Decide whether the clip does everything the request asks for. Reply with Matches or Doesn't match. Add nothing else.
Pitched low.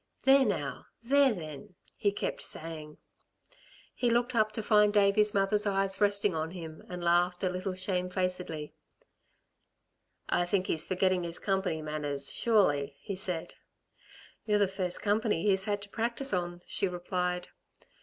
Doesn't match